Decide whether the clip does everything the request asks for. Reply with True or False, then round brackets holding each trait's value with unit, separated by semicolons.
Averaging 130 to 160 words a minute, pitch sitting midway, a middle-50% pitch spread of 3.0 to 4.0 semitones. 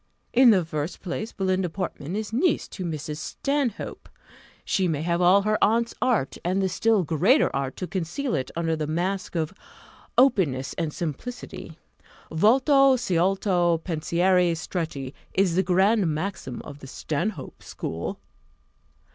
False (140 wpm; 180 Hz; 4.6 semitones)